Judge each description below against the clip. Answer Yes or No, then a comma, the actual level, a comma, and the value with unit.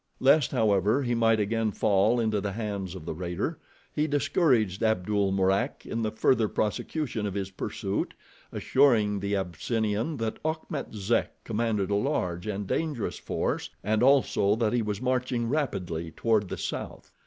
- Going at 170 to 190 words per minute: No, average, 155 wpm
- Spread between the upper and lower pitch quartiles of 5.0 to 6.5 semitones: No, average, 3.5 semitones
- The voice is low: Yes, low, 110 Hz